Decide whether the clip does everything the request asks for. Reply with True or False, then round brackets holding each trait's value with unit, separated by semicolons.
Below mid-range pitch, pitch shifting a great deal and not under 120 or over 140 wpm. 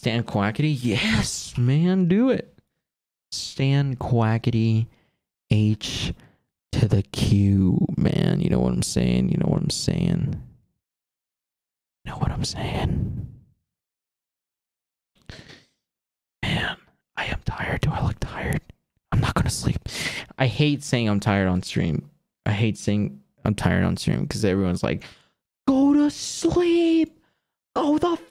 True (115 Hz; 7.2 semitones; 135 wpm)